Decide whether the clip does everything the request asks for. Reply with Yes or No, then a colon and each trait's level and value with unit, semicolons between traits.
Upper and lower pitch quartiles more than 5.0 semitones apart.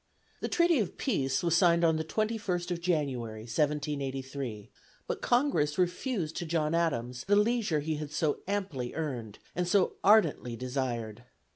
Yes: wide, 5.5 semitones